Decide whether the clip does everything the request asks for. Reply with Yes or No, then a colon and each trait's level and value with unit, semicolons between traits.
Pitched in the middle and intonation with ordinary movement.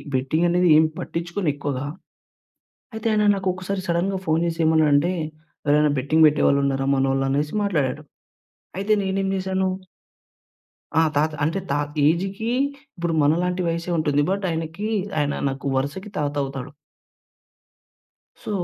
Yes: medium, 160 Hz; average, 4.5 semitones